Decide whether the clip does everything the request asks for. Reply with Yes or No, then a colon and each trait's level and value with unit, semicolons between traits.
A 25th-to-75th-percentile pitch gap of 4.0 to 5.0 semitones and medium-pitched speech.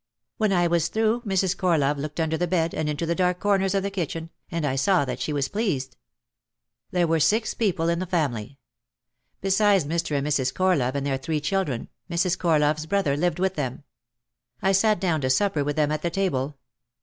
Yes: average, 4.5 semitones; medium, 165 Hz